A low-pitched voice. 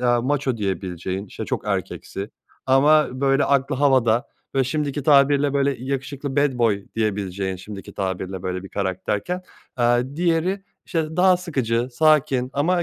Yes: low, 130 Hz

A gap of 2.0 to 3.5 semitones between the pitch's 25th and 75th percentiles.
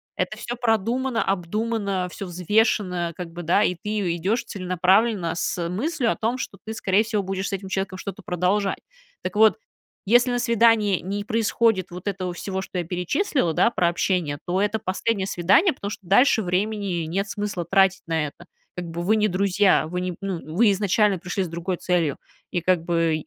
Yes: average, 3.2 semitones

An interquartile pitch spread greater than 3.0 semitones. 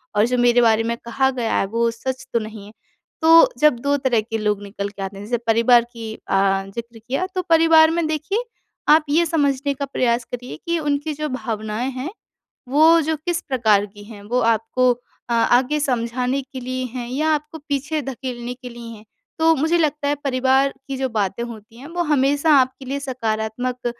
Yes: average, 4.0 semitones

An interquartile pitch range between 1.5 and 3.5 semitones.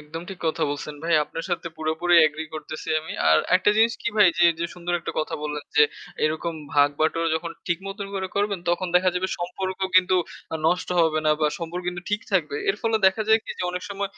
Yes: average, 3.2 semitones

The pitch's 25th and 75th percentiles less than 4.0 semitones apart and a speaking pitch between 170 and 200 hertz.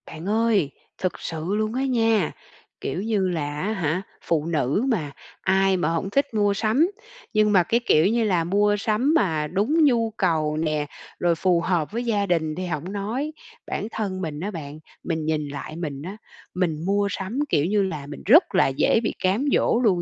No: average, 5.2 semitones; medium, 185 Hz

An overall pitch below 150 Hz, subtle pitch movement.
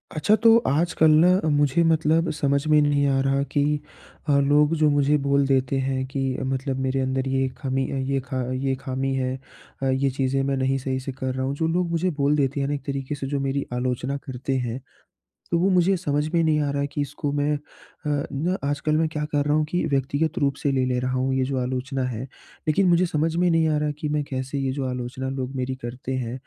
Yes: medium, 140 Hz; narrow, 2.2 semitones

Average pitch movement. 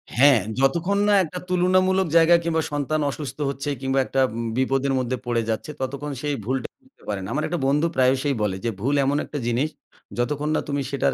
Yes: average, 3.2 semitones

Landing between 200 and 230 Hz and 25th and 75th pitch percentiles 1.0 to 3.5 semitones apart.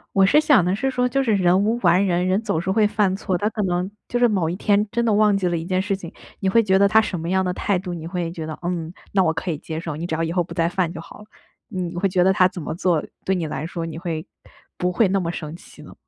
No: medium, 185 Hz; average, 3.0 semitones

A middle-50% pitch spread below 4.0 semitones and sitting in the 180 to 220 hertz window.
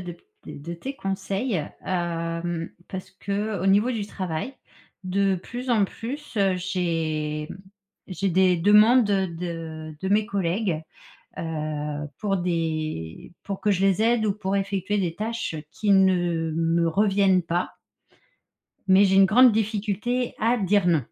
Yes: average, 3.6 semitones; high, 190 Hz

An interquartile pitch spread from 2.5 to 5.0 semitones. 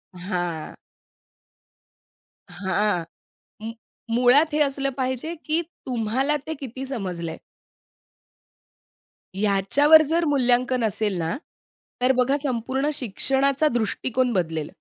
No: wide, 5.5 semitones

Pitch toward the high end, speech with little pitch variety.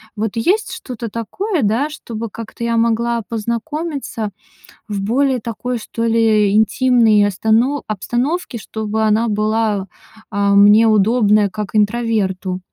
Yes: high, 225 Hz; narrow, 2.2 semitones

